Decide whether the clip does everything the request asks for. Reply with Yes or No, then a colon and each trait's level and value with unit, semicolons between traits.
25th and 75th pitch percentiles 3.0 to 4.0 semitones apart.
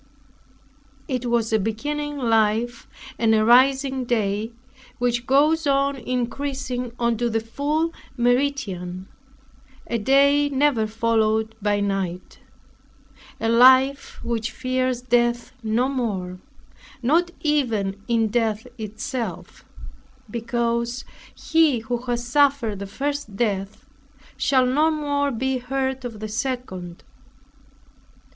Yes: average, 3.6 semitones